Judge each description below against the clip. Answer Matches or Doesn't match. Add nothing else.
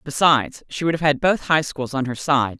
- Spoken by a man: Doesn't match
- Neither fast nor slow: Doesn't match